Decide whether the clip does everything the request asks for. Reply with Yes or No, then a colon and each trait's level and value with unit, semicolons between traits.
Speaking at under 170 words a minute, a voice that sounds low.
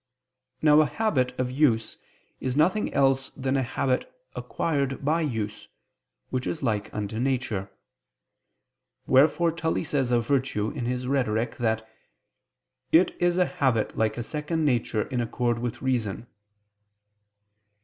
Yes: slow, 135 wpm; low, 130 Hz